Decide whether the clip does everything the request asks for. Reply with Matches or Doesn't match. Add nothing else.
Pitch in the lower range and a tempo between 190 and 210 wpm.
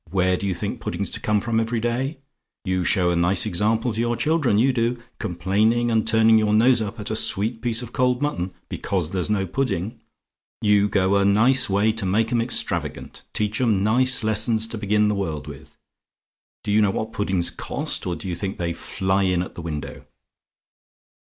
Matches